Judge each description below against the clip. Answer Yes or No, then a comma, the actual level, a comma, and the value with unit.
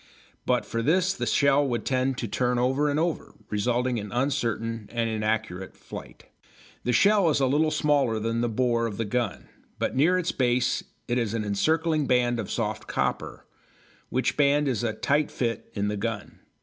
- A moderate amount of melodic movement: Yes, average, 4.0 semitones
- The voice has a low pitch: Yes, low, 120 Hz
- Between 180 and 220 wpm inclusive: Yes, average, 185 wpm